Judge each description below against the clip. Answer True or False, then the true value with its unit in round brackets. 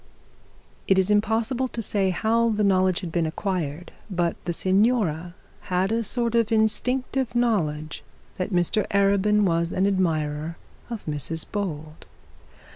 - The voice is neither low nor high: False (195 Hz)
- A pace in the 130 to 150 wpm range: True (135 wpm)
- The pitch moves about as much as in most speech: True (4.5 semitones)